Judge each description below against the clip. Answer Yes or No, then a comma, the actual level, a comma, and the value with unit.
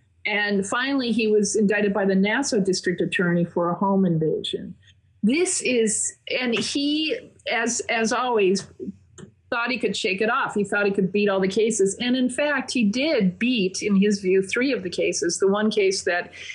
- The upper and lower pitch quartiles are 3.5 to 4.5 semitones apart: Yes, average, 3.9 semitones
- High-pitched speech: Yes, high, 210 Hz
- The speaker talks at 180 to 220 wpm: Yes, average, 190 wpm